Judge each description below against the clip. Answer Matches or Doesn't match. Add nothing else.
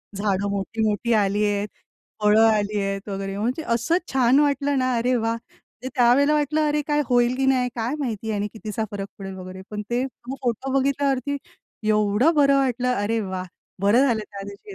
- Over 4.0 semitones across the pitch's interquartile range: Matches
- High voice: Matches